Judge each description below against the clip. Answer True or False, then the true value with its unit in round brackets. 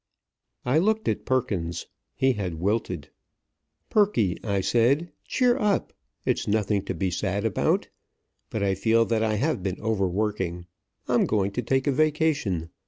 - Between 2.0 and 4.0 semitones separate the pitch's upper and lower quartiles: False (5.6 semitones)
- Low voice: True (110 Hz)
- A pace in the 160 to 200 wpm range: False (150 wpm)